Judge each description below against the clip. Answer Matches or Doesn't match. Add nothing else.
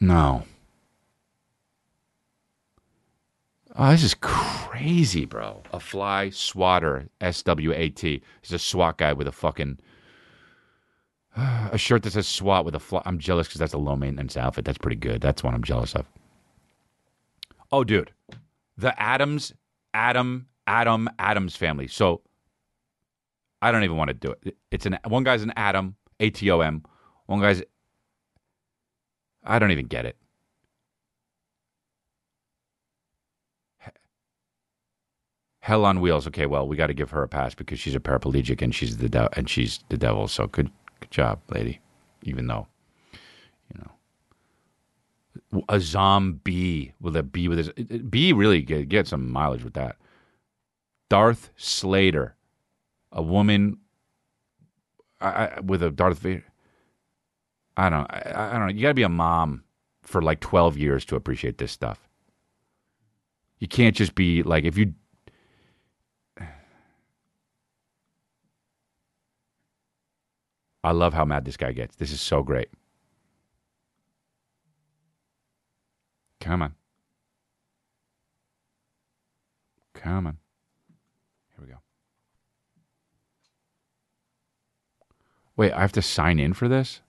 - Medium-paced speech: Doesn't match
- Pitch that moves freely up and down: Matches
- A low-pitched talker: Matches